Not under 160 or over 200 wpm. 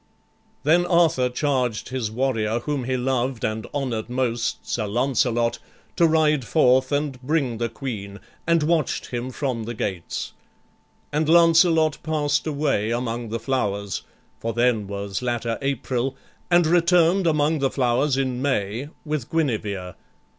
No: average, 140 wpm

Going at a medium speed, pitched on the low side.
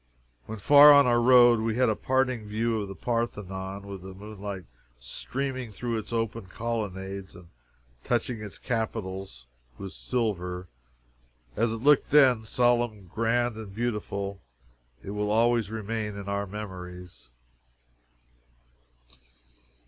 No: slow, 125 wpm; low, 110 Hz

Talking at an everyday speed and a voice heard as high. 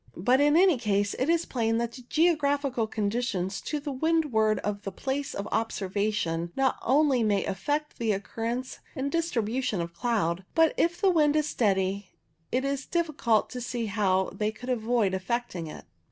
Yes: average, 175 wpm; high, 240 Hz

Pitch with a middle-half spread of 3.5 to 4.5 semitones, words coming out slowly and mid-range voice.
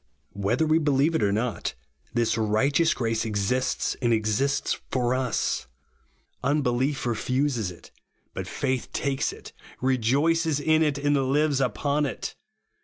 No: average, 4.1 semitones; slow, 130 wpm; low, 130 Hz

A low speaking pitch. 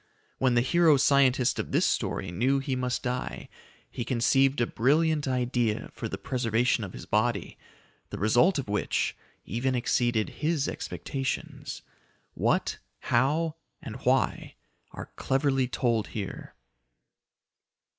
Yes: low, 130 Hz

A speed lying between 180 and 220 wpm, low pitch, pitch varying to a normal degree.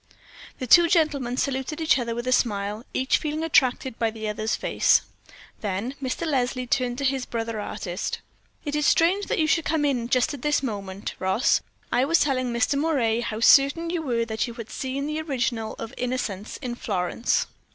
No: average, 190 wpm; very high, 255 Hz; average, 4.2 semitones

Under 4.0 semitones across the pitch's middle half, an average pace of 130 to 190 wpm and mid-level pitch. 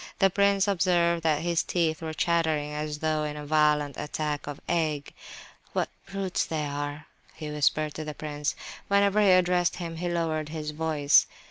Yes: narrow, 2.5 semitones; average, 175 wpm; medium, 155 Hz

